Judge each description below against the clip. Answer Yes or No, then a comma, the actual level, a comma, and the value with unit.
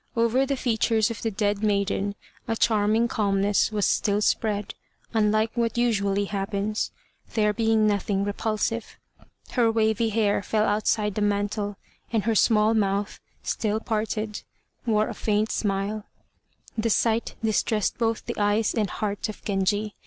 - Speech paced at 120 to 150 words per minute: Yes, average, 145 wpm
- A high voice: Yes, high, 215 Hz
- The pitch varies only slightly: Yes, narrow, 1.6 semitones